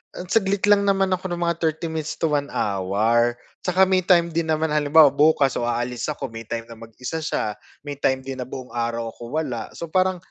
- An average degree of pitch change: No, wide, 6.1 semitones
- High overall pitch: No, medium, 150 Hz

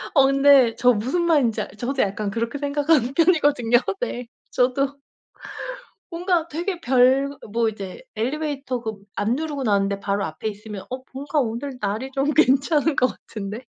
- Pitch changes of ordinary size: Yes, average, 4.5 semitones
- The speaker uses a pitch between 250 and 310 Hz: Yes, very high, 260 Hz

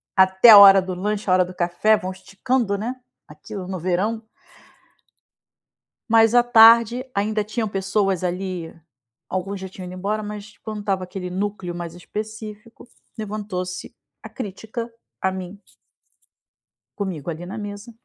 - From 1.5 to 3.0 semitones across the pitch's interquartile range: Yes, average, 2.7 semitones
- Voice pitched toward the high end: Yes, high, 200 Hz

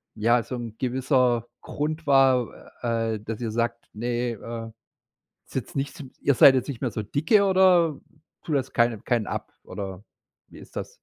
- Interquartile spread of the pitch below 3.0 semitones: No, average, 3.3 semitones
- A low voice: Yes, low, 120 Hz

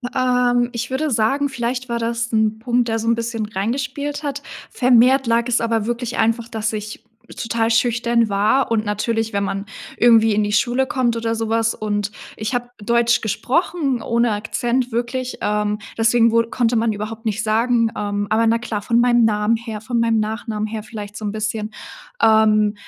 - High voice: Yes, high, 230 Hz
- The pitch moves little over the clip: Yes, narrow, 1.9 semitones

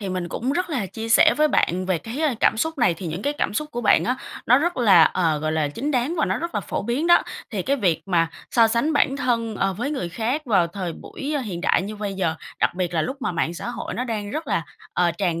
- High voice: Yes, high, 220 Hz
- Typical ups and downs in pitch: No, wide, 7.3 semitones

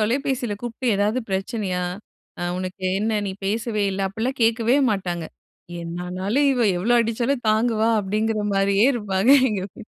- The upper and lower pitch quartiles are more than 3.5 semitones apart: No, average, 3.2 semitones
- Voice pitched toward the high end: Yes, high, 215 Hz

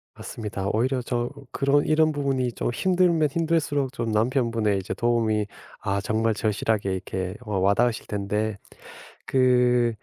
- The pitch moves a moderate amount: Yes, average, 4.2 semitones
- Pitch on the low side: Yes, low, 120 Hz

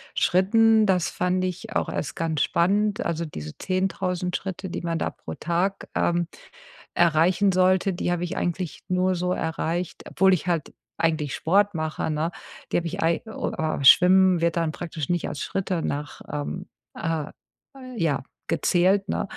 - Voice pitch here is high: No, medium, 175 Hz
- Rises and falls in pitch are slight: Yes, narrow, 2.3 semitones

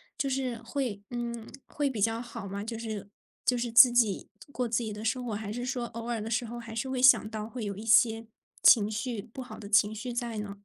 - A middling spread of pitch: No, narrow, 2.1 semitones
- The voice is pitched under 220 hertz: No, high, 230 Hz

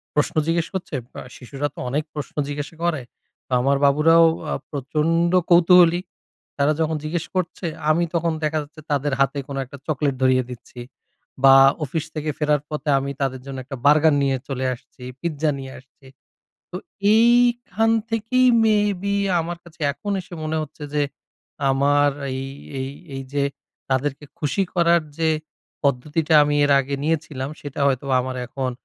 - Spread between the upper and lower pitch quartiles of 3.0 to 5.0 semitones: Yes, average, 3.4 semitones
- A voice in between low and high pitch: Yes, medium, 150 Hz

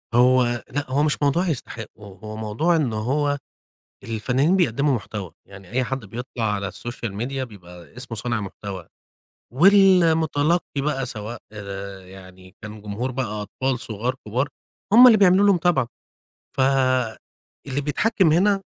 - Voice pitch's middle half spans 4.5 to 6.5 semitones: Yes, wide, 5.6 semitones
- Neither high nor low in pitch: No, low, 125 Hz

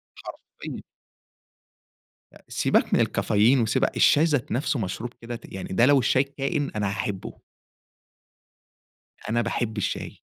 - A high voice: No, low, 120 Hz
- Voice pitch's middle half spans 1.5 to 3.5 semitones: No, average, 4.1 semitones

